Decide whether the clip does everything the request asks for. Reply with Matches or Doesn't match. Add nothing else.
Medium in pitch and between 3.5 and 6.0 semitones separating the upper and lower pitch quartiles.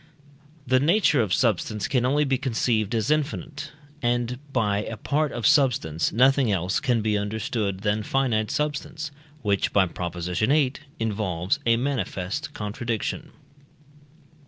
Doesn't match